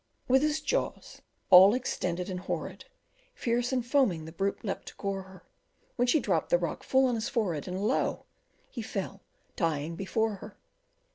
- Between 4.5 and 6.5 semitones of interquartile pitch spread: Yes, average, 5.3 semitones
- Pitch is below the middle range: No, high, 205 Hz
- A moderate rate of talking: Yes, average, 170 wpm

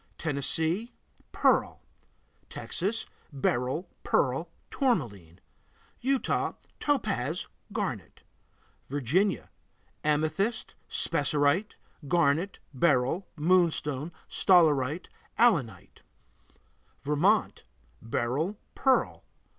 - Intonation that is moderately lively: No, wide, 6.3 semitones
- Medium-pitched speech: Yes, medium, 160 Hz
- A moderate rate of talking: No, slow, 60 wpm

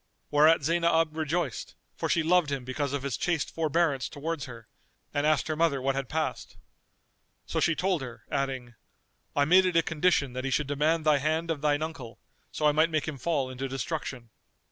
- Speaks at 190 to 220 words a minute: Yes, average, 195 wpm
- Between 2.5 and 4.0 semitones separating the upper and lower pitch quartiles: Yes, average, 3.2 semitones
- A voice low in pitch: No, medium, 150 Hz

